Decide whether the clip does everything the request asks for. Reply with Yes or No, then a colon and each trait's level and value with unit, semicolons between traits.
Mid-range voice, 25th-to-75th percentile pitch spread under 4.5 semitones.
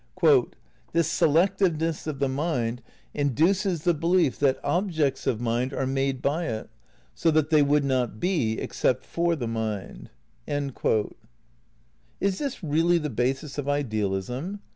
No: medium, 145 Hz; average, 5.3 semitones